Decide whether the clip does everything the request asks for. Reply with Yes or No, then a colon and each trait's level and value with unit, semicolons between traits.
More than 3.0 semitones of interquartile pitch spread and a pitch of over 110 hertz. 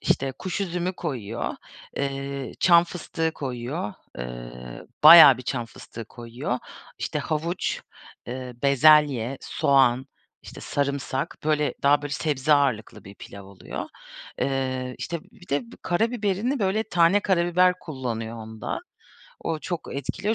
Yes: wide, 5.5 semitones; medium, 140 Hz